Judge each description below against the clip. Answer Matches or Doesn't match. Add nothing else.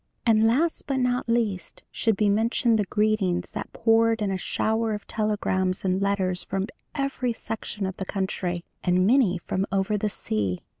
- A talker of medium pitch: Doesn't match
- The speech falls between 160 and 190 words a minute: Matches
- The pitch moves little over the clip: Doesn't match